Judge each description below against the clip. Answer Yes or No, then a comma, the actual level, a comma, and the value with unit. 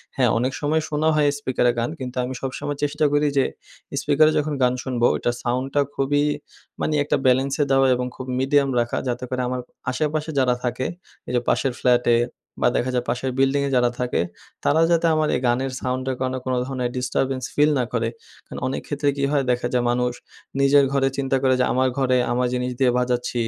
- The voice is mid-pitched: No, low, 130 Hz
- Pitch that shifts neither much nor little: No, narrow, 2.1 semitones